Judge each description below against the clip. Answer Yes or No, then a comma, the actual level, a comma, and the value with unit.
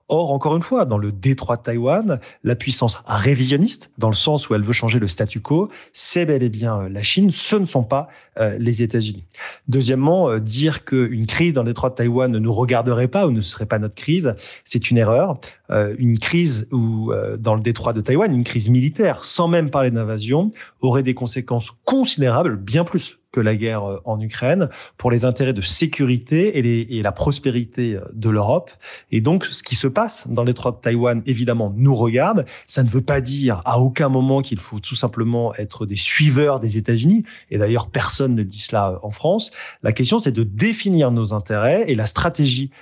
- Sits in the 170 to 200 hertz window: No, low, 125 Hz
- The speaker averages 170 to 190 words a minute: No, average, 205 wpm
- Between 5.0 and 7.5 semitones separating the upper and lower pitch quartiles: No, average, 3.8 semitones